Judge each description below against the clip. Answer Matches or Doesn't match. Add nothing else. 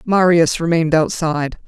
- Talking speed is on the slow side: Matches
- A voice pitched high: Doesn't match